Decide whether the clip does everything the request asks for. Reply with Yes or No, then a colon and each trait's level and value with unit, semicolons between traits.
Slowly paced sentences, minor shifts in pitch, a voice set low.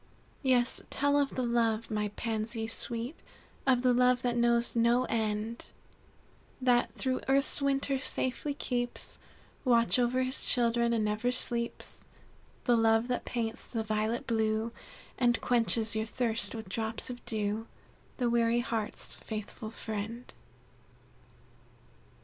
No: slow, 130 wpm; narrow, 2.0 semitones; high, 235 Hz